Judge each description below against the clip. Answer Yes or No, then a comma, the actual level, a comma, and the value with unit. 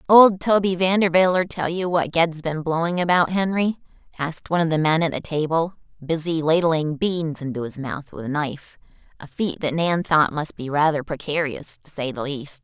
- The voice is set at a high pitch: No, medium, 160 Hz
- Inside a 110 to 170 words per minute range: No, average, 195 wpm